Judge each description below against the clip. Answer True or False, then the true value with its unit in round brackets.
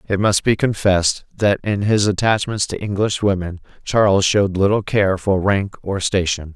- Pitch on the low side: True (100 Hz)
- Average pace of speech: True (175 wpm)